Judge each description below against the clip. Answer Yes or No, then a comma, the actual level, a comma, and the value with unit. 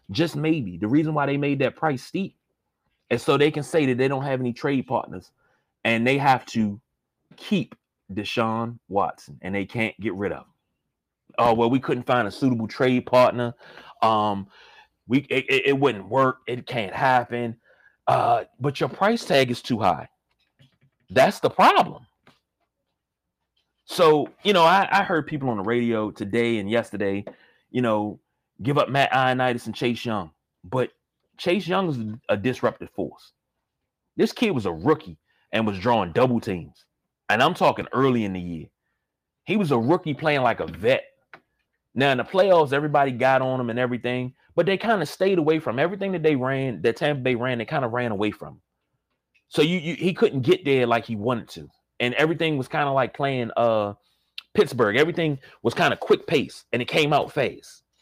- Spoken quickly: No, average, 190 wpm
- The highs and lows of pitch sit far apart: No, average, 4.5 semitones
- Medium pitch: No, low, 130 Hz